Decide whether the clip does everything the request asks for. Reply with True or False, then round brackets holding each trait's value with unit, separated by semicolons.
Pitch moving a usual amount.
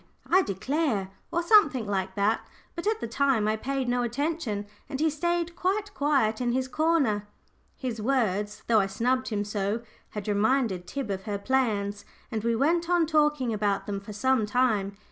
False (6.1 semitones)